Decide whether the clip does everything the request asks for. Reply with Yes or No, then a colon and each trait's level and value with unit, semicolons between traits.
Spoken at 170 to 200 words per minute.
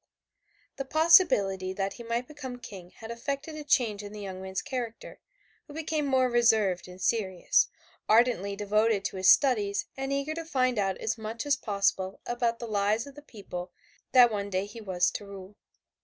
Yes: average, 185 wpm